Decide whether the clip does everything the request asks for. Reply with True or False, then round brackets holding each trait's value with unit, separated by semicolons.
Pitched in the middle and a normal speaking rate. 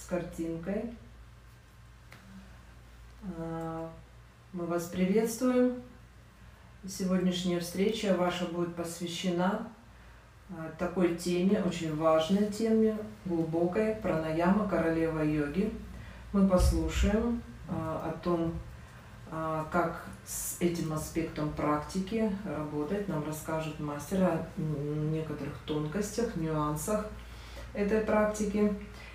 False (175 Hz; 80 wpm)